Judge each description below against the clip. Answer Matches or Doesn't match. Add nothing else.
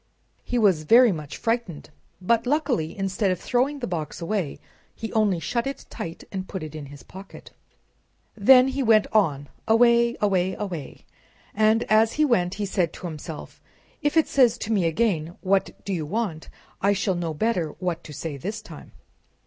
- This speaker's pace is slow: Doesn't match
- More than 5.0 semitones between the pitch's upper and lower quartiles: Matches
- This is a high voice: Matches